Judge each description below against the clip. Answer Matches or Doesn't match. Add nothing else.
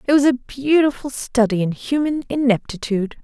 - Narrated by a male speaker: Doesn't match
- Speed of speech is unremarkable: Matches